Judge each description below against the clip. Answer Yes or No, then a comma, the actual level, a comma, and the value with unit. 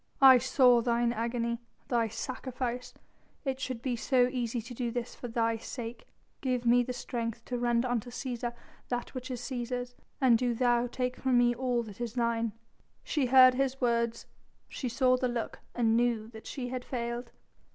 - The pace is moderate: Yes, average, 180 wpm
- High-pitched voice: Yes, high, 245 Hz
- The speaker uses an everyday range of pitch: No, narrow, 1.3 semitones